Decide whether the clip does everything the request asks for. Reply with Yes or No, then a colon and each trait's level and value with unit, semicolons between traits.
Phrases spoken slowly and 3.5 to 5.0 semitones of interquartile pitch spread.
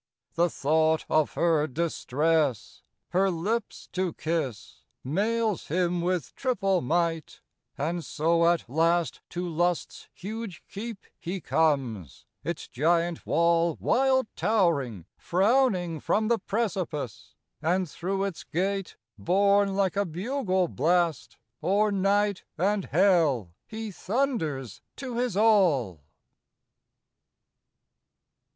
Yes: slow, 105 wpm; average, 3.9 semitones